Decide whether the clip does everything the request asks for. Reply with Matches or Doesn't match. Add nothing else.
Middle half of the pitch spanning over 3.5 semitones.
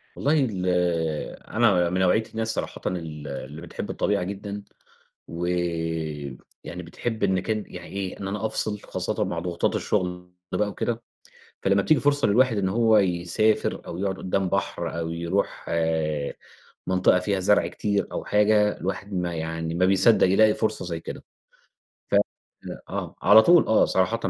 Doesn't match